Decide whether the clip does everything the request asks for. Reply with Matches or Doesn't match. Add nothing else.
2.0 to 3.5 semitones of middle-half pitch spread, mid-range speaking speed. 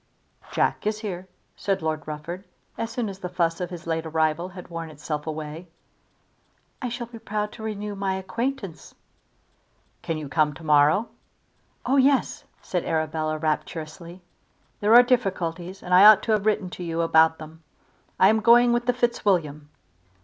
Doesn't match